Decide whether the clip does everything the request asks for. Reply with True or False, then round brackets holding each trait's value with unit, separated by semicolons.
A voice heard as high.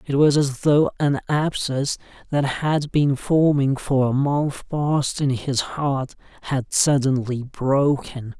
False (140 Hz)